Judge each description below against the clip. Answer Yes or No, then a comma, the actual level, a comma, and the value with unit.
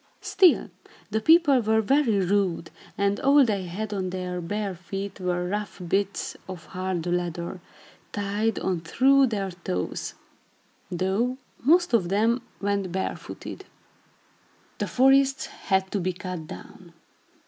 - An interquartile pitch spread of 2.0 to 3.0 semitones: No, average, 3.7 semitones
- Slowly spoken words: Yes, slow, 130 wpm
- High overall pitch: Yes, high, 200 Hz